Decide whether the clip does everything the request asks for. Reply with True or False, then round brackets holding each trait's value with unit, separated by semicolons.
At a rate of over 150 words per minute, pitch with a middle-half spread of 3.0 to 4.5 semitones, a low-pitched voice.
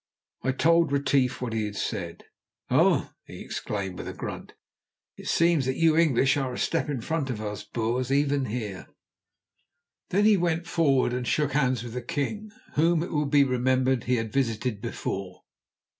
True (175 wpm; 4.2 semitones; 130 Hz)